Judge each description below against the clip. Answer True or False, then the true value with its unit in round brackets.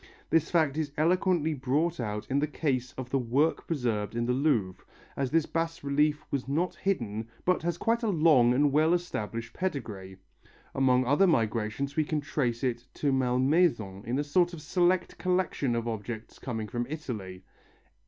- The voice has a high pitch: False (140 Hz)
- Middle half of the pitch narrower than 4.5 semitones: False (5.5 semitones)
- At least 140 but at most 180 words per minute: True (175 wpm)